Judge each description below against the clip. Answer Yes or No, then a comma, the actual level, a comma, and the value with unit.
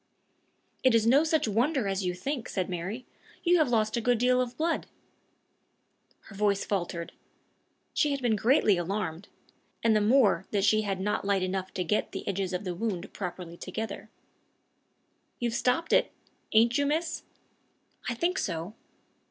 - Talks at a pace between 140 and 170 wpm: Yes, average, 165 wpm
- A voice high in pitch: Yes, high, 215 Hz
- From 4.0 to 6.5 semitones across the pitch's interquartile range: Yes, average, 4.7 semitones